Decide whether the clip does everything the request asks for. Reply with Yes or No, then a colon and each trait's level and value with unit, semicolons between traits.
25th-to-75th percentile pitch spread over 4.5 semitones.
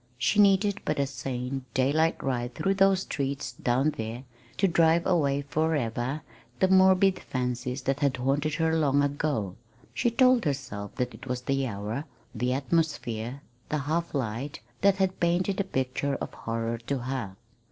Yes: average, 5.0 semitones